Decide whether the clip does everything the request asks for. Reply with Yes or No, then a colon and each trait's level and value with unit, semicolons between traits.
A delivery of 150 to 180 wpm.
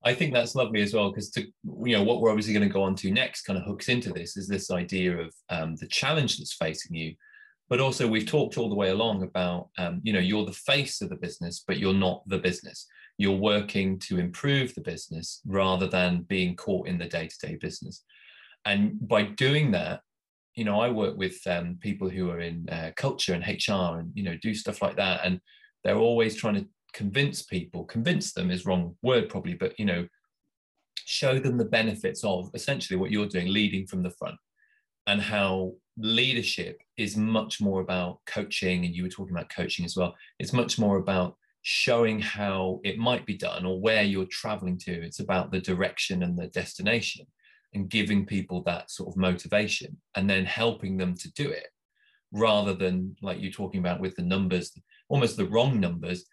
No: fast, 205 wpm